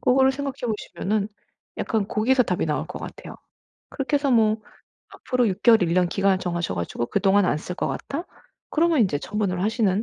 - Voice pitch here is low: No, high, 210 Hz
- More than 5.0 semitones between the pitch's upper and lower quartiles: Yes, wide, 5.5 semitones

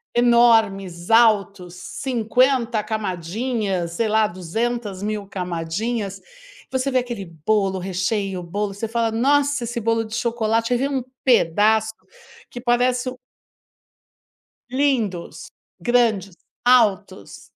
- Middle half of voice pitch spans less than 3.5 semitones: No, average, 3.8 semitones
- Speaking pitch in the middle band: No, high, 220 Hz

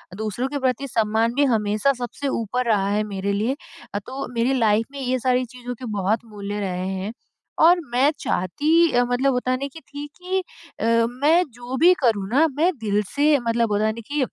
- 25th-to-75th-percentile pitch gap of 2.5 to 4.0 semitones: No, average, 4.5 semitones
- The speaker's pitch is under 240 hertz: No, high, 245 Hz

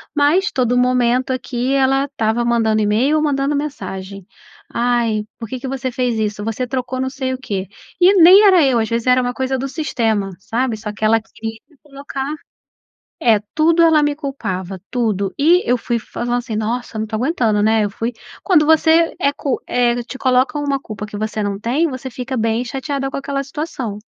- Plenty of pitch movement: No, average, 3.9 semitones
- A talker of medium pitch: No, very high, 250 Hz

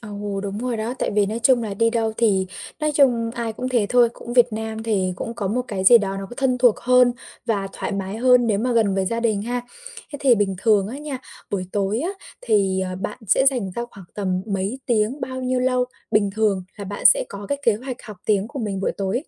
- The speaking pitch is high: Yes, high, 220 Hz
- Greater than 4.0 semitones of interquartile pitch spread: No, average, 3.7 semitones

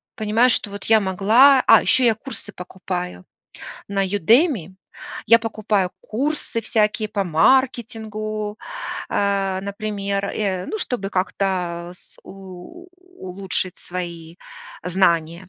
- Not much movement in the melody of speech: No, average, 3.2 semitones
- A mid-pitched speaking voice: No, high, 200 Hz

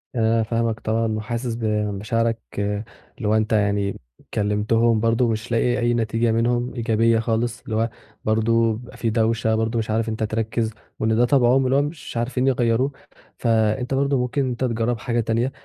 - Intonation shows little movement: Yes, narrow, 1.5 semitones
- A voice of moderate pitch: No, low, 115 Hz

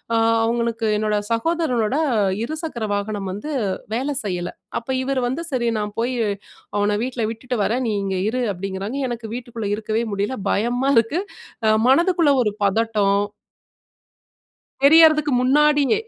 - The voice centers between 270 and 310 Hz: No, high, 235 Hz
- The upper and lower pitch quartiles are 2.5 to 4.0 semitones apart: No, average, 4.4 semitones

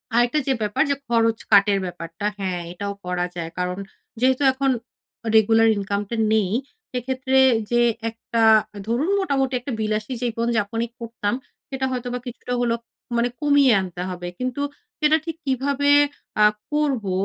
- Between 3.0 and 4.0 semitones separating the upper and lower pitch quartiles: No, average, 4.4 semitones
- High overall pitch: Yes, high, 235 Hz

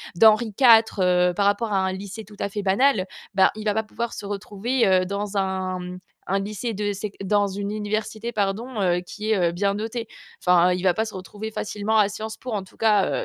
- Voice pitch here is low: No, high, 205 Hz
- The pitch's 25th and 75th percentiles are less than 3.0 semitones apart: Yes, narrow, 2.4 semitones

